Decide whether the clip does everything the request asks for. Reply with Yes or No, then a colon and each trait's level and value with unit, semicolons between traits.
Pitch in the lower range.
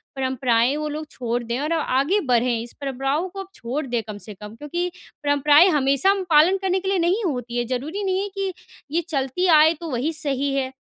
No: very high, 290 Hz